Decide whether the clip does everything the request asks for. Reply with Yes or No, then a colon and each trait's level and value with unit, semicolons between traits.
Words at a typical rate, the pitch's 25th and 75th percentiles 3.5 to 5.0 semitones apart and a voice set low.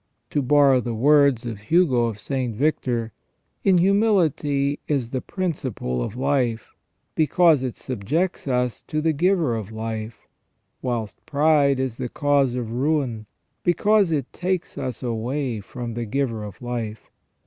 Yes: average, 145 wpm; average, 4.6 semitones; low, 130 Hz